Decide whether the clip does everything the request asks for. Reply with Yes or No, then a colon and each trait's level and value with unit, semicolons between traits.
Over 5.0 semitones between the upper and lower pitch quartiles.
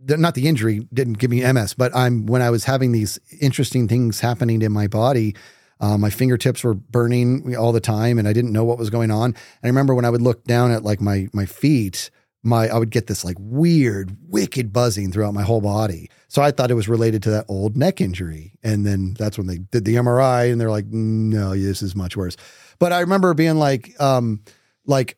No: average, 3.3 semitones